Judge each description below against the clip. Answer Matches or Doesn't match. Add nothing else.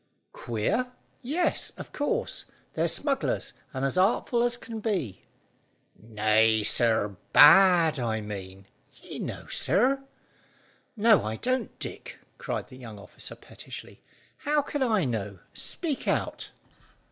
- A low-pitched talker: Doesn't match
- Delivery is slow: Matches